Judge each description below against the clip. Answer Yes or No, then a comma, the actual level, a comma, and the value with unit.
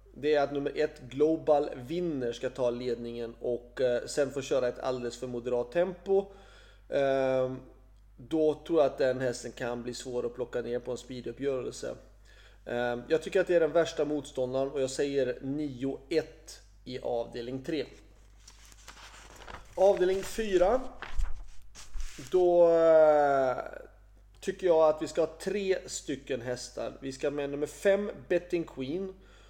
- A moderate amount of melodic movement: Yes, average, 4.9 semitones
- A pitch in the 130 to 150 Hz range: Yes, low, 135 Hz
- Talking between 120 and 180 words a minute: Yes, average, 140 wpm